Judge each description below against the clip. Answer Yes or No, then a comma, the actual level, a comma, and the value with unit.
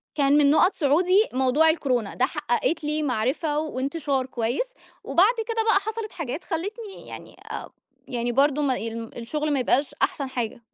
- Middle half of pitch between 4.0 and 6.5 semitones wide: Yes, average, 4.6 semitones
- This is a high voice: Yes, very high, 290 Hz